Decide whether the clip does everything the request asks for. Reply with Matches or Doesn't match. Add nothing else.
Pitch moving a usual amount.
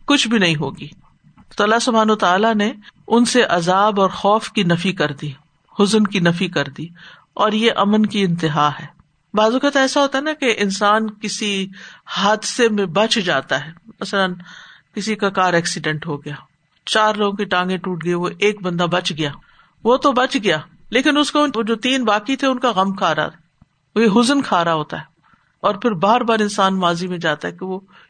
Matches